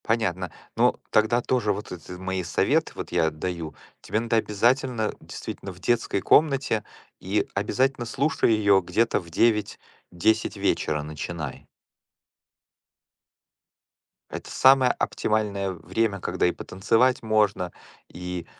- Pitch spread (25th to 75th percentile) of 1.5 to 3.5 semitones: No, average, 4.3 semitones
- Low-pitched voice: Yes, low, 105 Hz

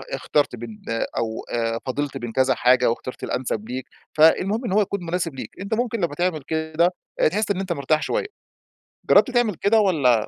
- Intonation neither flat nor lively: No, wide, 7.6 semitones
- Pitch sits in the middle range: Yes, medium, 155 Hz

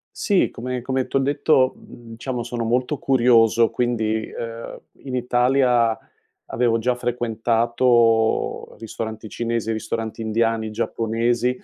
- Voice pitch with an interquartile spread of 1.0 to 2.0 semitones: Yes, narrow, 1.7 semitones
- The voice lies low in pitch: Yes, low, 120 Hz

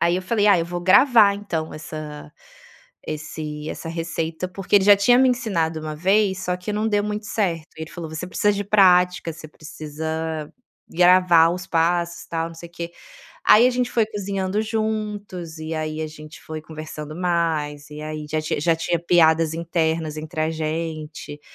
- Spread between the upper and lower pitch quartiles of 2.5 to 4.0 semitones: Yes, average, 3.6 semitones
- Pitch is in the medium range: Yes, medium, 170 Hz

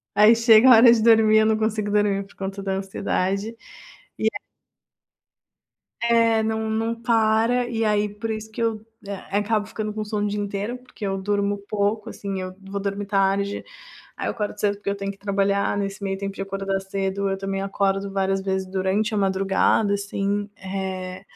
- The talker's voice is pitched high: Yes, high, 200 Hz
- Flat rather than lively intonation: Yes, narrow, 1.9 semitones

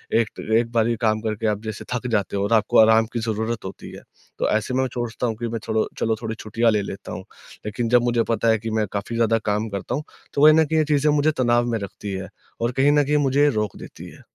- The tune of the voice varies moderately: No, narrow, 2.2 semitones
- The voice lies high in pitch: No, low, 115 Hz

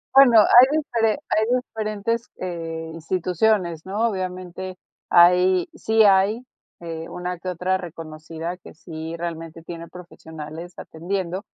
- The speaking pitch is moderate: Yes, medium, 180 Hz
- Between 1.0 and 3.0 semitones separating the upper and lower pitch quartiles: No, average, 3.8 semitones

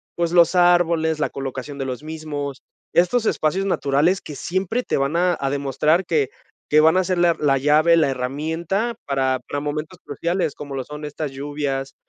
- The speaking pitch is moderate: Yes, medium, 155 Hz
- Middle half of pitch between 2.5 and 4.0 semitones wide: Yes, average, 3.6 semitones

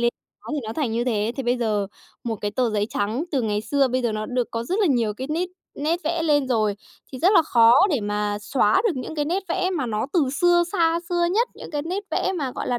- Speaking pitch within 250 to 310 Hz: Yes, very high, 255 Hz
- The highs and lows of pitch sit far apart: Yes, wide, 6.8 semitones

